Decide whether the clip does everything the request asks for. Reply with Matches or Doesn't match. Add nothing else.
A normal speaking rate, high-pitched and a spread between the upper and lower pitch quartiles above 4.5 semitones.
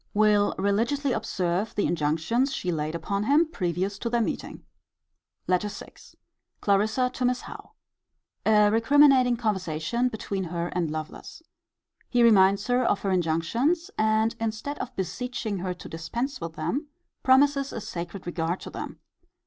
Matches